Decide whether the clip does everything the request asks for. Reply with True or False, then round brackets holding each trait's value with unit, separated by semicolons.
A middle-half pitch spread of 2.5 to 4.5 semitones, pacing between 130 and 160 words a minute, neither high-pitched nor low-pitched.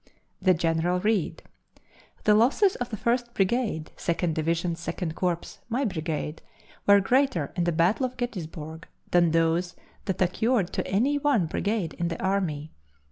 False (5.4 semitones; 150 wpm; 180 Hz)